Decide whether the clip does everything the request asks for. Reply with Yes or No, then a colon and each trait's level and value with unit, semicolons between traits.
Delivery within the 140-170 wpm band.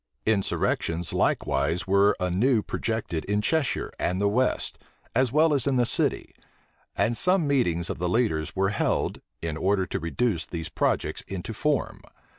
Yes: average, 155 wpm